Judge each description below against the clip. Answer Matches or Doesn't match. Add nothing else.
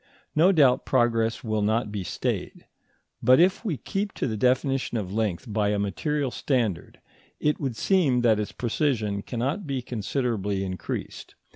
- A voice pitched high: Doesn't match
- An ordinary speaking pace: Matches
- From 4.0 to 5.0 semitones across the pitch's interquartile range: Matches